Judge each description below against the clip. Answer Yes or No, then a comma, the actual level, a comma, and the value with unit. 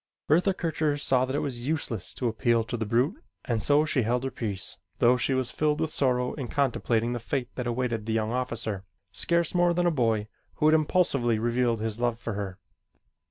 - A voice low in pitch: Yes, low, 125 Hz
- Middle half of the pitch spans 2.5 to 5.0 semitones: Yes, average, 4.2 semitones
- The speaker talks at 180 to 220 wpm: Yes, fast, 205 wpm